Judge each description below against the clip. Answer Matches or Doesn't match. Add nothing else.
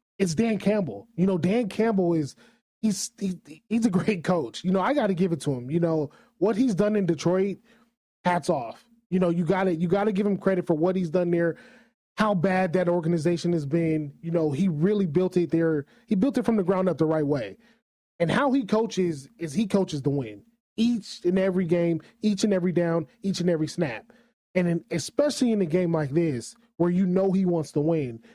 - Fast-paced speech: Matches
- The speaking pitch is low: Doesn't match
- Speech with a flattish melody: Doesn't match